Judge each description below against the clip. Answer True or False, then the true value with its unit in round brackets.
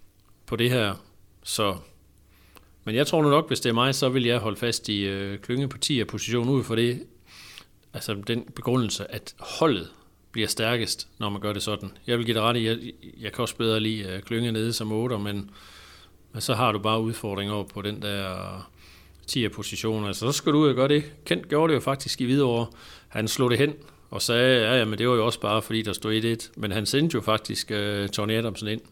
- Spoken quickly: True (230 wpm)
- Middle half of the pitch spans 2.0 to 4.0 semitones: True (3.2 semitones)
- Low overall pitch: True (110 Hz)